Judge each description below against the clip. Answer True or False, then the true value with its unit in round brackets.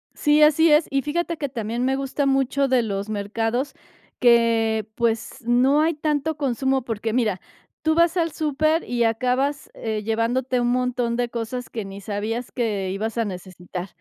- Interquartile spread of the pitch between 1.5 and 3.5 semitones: False (4.0 semitones)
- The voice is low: False (245 Hz)